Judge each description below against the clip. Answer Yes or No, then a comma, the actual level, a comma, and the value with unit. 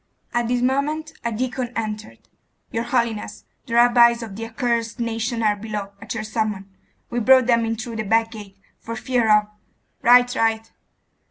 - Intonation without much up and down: Yes, narrow, 1.8 semitones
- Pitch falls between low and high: No, high, 230 Hz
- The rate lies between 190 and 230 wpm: No, average, 175 wpm